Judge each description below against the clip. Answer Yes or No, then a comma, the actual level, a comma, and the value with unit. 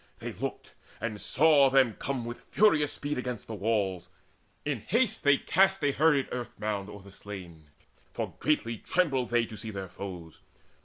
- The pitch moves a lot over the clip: Yes, wide, 6.3 semitones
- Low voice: Yes, low, 120 Hz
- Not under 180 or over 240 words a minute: No, average, 170 wpm